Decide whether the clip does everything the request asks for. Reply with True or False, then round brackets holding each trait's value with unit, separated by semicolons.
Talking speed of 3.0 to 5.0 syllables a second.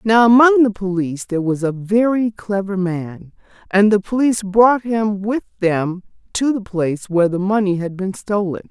True (4.9 syllables/s)